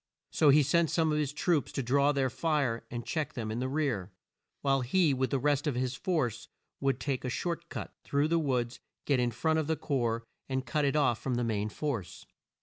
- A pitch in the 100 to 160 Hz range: Yes, low, 135 Hz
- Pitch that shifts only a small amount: No, average, 3.7 semitones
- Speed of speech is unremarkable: No, fast, 225 wpm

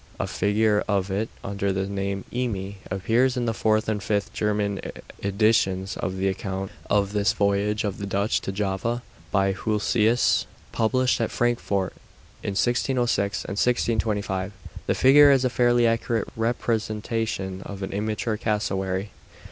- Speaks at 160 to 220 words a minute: No, average, 145 wpm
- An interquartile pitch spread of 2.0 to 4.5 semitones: Yes, average, 2.7 semitones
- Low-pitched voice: Yes, low, 105 Hz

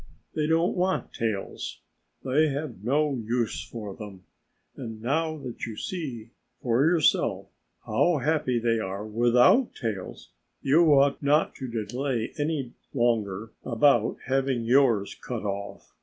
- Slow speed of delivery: Yes, slow, 130 wpm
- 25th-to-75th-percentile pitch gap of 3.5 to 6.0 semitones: Yes, average, 4.5 semitones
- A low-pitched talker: Yes, low, 125 Hz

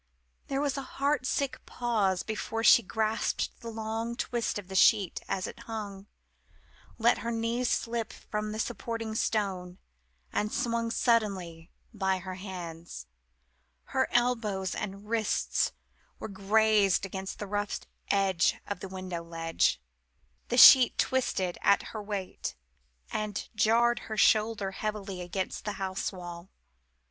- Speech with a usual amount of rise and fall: Yes, average, 3.2 semitones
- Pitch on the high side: Yes, high, 210 Hz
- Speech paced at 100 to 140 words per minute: Yes, slow, 135 wpm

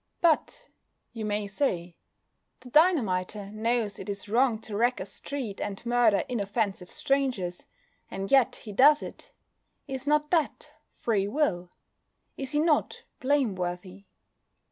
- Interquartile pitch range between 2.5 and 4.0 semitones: No, wide, 5.6 semitones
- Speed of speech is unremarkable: No, slow, 130 wpm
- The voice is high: Yes, high, 225 Hz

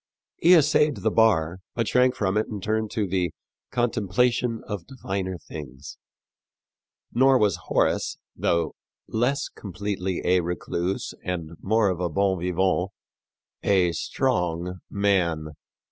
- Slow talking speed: Yes, slow, 125 wpm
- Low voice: Yes, very low, 95 Hz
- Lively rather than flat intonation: No, average, 4.1 semitones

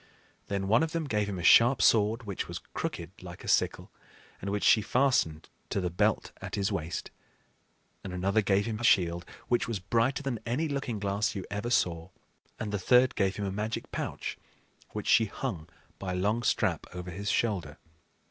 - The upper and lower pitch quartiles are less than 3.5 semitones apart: No, average, 3.9 semitones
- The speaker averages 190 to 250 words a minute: Yes, average, 195 wpm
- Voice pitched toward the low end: Yes, low, 105 Hz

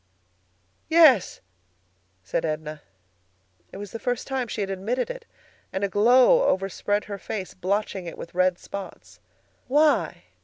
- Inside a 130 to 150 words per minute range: Yes, average, 140 wpm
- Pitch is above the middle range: Yes, high, 205 Hz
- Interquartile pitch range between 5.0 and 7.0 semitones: Yes, average, 5.3 semitones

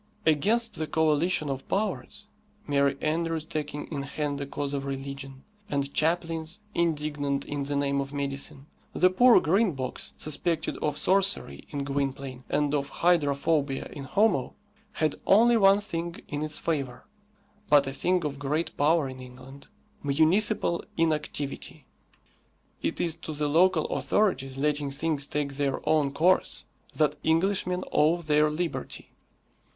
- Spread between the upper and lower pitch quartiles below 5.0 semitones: Yes, average, 3.3 semitones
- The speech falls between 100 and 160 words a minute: Yes, average, 140 wpm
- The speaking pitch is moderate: Yes, medium, 150 Hz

